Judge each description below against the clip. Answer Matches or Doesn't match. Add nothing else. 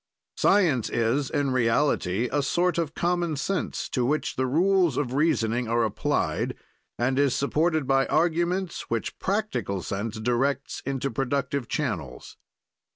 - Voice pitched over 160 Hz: Doesn't match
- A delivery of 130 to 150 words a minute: Matches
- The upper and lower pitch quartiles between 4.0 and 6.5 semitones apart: Matches